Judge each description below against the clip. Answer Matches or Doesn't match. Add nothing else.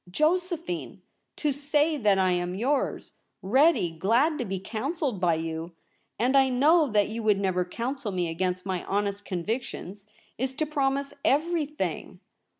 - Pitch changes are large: Matches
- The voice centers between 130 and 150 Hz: Doesn't match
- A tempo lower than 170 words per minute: Matches